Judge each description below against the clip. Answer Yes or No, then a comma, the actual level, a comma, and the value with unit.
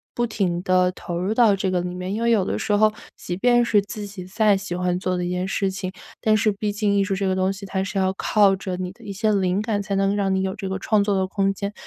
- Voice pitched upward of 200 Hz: No, high, 195 Hz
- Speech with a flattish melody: Yes, narrow, 1.8 semitones